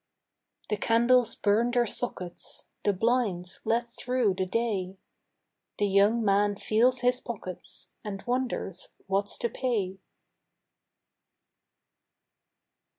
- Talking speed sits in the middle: No, slow, 100 wpm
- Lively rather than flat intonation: No, average, 3.5 semitones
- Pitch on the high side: Yes, high, 215 Hz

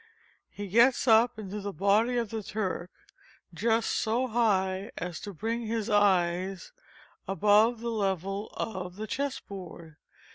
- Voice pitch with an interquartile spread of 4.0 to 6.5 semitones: No, average, 3.1 semitones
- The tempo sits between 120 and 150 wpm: Yes, average, 140 wpm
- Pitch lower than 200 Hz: No, high, 205 Hz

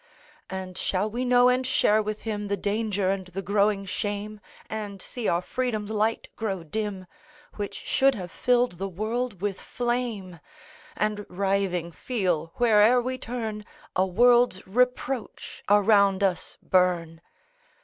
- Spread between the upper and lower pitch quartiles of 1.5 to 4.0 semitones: Yes, average, 3.6 semitones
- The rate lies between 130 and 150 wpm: Yes, average, 140 wpm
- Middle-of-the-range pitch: No, high, 205 Hz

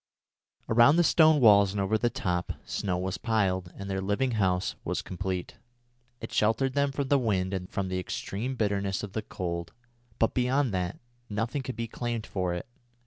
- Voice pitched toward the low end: Yes, low, 105 Hz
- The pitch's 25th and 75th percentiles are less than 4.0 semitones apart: No, average, 4.3 semitones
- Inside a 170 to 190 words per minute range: Yes, average, 185 wpm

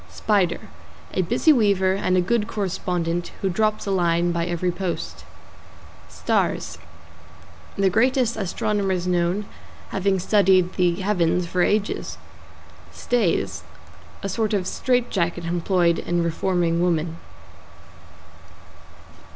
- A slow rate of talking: Yes, slow, 110 wpm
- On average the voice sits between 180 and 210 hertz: Yes, medium, 185 Hz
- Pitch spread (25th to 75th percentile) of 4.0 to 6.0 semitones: No, average, 2.8 semitones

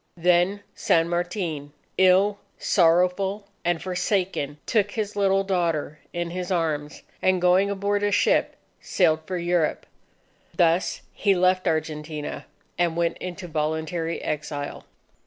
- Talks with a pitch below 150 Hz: No, medium, 175 Hz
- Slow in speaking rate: Yes, slow, 120 wpm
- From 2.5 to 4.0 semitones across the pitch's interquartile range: Yes, average, 2.8 semitones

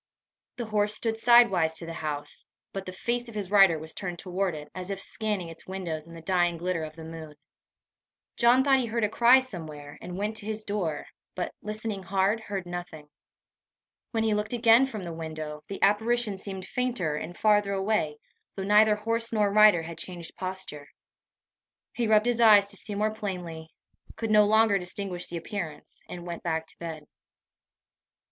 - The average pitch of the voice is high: Yes, high, 195 Hz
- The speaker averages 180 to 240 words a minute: Yes, average, 185 wpm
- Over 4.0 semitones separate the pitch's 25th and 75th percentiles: Yes, average, 4.4 semitones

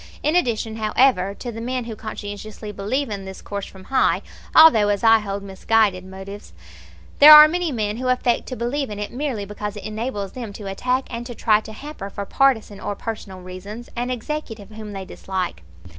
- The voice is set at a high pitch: Yes, high, 215 Hz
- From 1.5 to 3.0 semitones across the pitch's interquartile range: No, average, 3.8 semitones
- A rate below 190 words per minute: No, average, 195 wpm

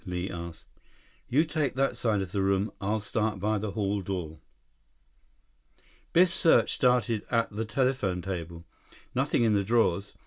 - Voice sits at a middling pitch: No, low, 105 Hz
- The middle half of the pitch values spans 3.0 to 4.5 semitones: Yes, average, 3.8 semitones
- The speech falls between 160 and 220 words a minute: No, average, 150 wpm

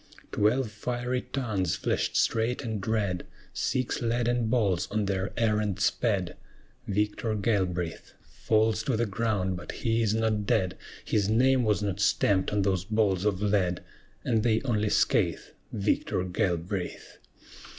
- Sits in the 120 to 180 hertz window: No, low, 105 Hz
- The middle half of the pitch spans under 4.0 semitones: Yes, average, 2.8 semitones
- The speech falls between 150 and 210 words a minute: No, average, 140 wpm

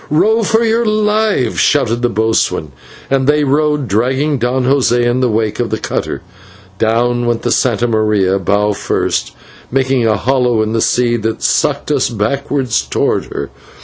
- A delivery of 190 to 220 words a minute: No, average, 165 wpm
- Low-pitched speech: Yes, low, 120 Hz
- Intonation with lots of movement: No, average, 3.8 semitones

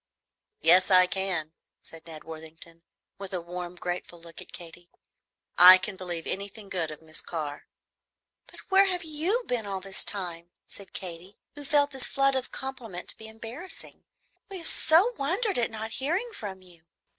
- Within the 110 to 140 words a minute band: No, average, 170 wpm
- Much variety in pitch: Yes, wide, 7.6 semitones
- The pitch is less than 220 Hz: Yes, high, 190 Hz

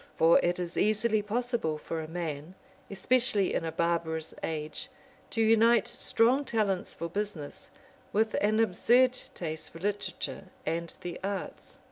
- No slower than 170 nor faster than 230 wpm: No, average, 140 wpm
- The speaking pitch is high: Yes, high, 195 Hz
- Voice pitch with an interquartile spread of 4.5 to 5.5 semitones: Yes, average, 5.2 semitones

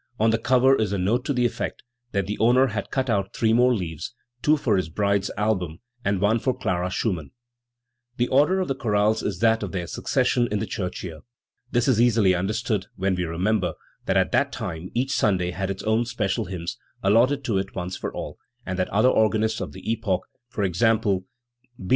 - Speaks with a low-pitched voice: Yes, low, 105 Hz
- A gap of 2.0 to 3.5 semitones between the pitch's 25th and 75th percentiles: No, average, 3.9 semitones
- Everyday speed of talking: No, fast, 210 wpm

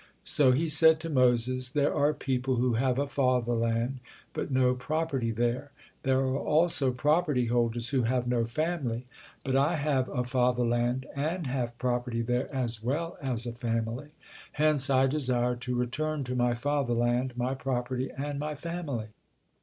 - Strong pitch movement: No, average, 2.9 semitones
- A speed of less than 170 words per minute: Yes, average, 160 wpm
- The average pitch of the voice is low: Yes, low, 130 Hz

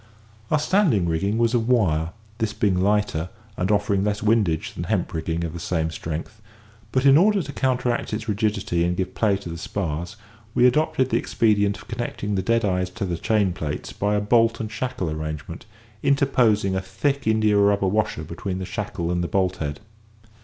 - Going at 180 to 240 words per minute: Yes, average, 190 wpm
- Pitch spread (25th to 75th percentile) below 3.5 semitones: No, average, 4.5 semitones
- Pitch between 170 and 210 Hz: No, low, 100 Hz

